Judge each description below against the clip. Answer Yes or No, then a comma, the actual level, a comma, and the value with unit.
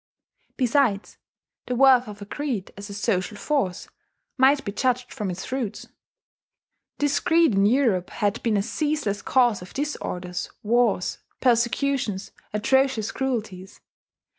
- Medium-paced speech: No, slow, 130 wpm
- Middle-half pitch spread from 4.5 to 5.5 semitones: Yes, average, 4.8 semitones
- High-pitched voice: Yes, high, 235 Hz